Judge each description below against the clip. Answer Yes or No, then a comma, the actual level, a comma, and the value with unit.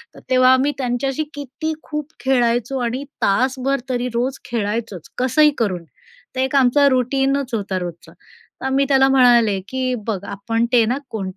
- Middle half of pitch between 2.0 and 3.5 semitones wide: Yes, average, 2.9 semitones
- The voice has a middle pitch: No, very high, 255 Hz